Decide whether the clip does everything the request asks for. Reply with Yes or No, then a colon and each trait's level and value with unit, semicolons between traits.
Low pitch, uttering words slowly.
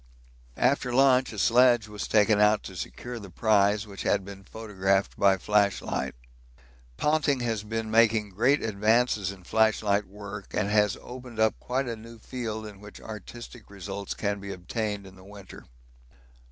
No: low, 105 Hz; average, 160 wpm